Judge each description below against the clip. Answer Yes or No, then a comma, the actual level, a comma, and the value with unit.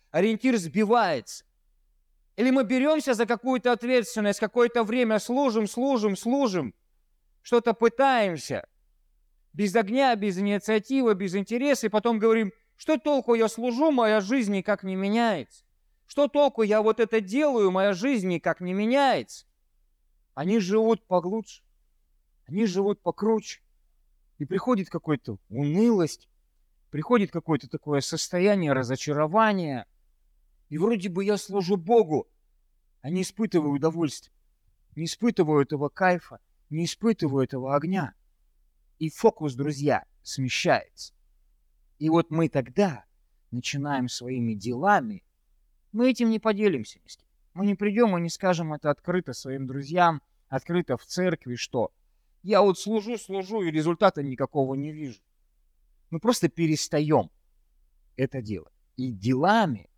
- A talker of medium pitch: Yes, medium, 175 Hz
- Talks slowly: No, average, 120 wpm